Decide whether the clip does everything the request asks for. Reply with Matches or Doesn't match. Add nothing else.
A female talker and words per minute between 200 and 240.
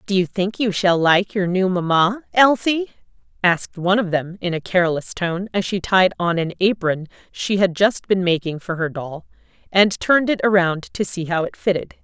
Matches